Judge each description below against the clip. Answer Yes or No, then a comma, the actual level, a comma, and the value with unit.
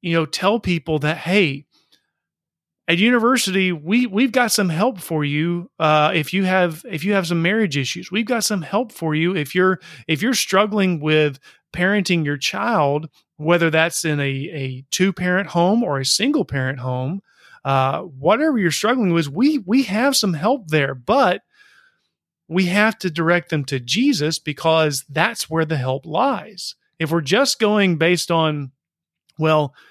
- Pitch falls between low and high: Yes, medium, 175 Hz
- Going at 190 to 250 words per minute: No, average, 170 wpm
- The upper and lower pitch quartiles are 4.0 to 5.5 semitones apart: Yes, average, 5.0 semitones